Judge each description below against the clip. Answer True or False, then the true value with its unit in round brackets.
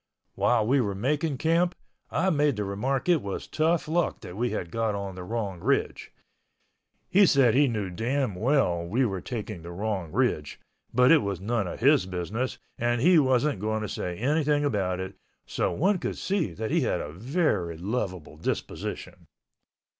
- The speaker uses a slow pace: False (175 wpm)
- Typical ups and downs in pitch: False (7.0 semitones)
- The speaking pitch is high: False (115 Hz)